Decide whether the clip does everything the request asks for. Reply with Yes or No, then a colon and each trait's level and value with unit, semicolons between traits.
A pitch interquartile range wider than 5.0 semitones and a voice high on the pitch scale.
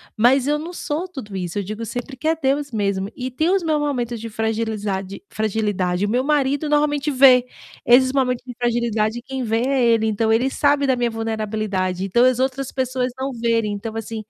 No: average, 3.8 semitones; high, 240 Hz